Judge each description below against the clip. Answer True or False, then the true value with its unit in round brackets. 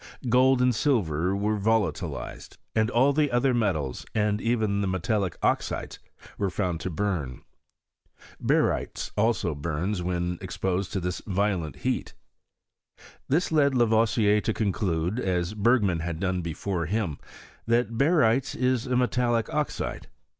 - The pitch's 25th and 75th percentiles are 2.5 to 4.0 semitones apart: False (5.0 semitones)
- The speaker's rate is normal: False (130 wpm)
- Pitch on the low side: True (105 Hz)